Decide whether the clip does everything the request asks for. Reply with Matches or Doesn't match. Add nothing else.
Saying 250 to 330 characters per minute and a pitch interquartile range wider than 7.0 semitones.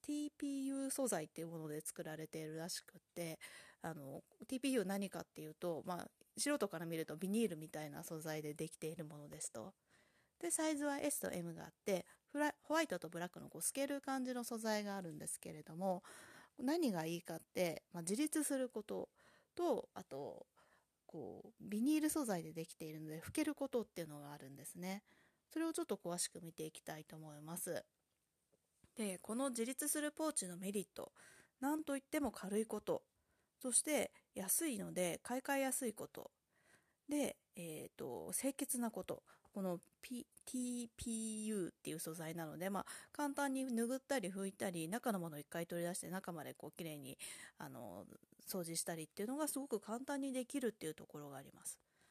Doesn't match